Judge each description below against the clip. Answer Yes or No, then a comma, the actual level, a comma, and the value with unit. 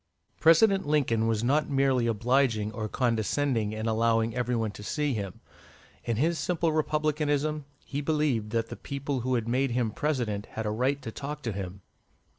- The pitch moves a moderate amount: Yes, average, 4.6 semitones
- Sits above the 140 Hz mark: No, low, 125 Hz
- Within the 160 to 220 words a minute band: Yes, average, 180 wpm